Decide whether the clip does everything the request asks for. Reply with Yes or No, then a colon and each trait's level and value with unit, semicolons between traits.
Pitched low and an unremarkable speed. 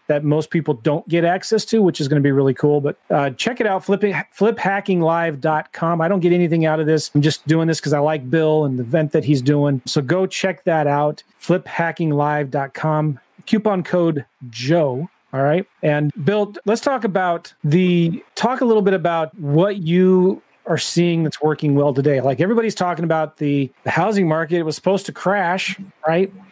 No: medium, 165 Hz; average, 190 wpm